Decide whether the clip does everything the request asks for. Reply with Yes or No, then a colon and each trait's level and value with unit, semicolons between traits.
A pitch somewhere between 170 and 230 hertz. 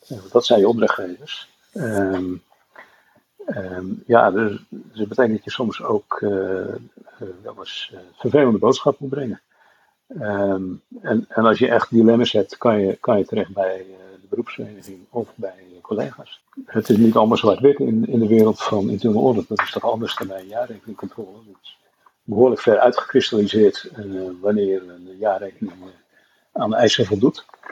No: low, 100 Hz